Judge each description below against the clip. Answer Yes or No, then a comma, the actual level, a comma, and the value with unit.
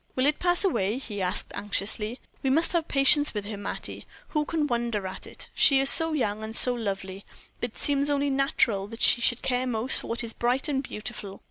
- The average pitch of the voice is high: Yes, high, 240 Hz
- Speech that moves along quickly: Yes, fast, 215 wpm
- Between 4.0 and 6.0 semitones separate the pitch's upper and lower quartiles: Yes, average, 5.0 semitones